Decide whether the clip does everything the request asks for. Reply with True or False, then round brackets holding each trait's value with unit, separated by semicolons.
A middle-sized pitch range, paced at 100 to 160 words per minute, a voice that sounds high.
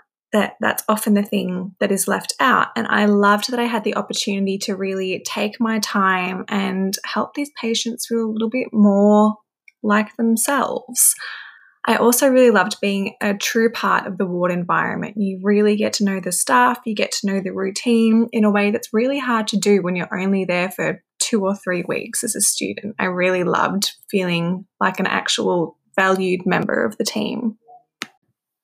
False (3.0 semitones; 190 wpm; 210 Hz)